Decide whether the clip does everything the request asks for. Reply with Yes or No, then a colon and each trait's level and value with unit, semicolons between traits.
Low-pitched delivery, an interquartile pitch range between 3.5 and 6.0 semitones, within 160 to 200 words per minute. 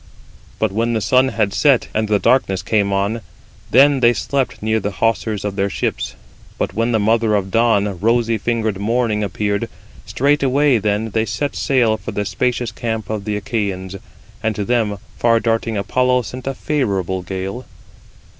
No: low, 110 Hz; average, 2.8 semitones; average, 170 wpm